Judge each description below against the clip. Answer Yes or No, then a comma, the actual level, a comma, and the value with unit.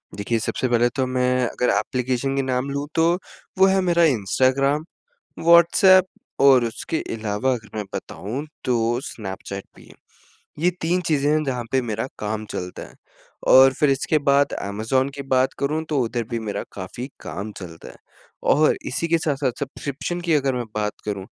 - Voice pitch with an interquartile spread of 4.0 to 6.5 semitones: Yes, average, 4.4 semitones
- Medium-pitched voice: No, low, 130 Hz